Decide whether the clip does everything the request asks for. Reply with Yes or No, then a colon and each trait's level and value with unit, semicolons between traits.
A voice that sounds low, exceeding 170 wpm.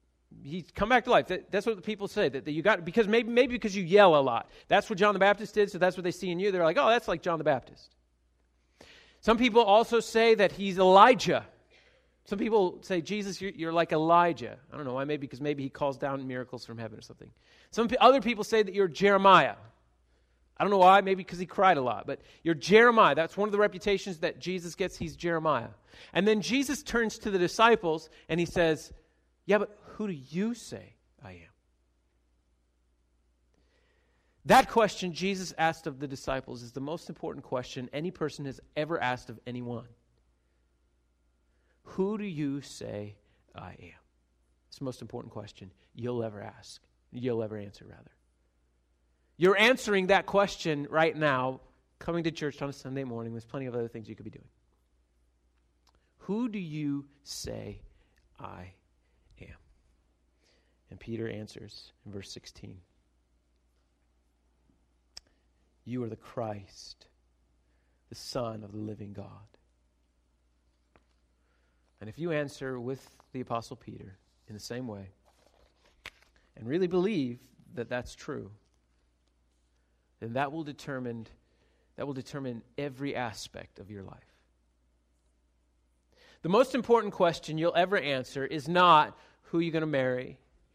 No: low, 125 Hz; average, 160 wpm